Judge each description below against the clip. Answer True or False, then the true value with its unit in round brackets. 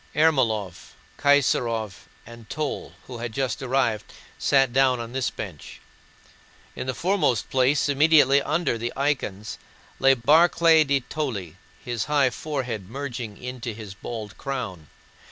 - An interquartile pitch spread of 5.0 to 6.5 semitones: False (4.0 semitones)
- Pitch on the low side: True (125 Hz)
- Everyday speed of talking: False (130 wpm)